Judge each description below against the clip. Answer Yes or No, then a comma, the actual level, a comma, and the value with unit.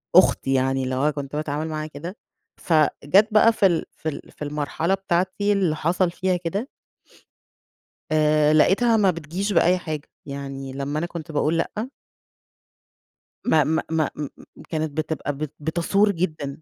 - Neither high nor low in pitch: Yes, medium, 160 Hz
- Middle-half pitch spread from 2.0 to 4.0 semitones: Yes, average, 3.7 semitones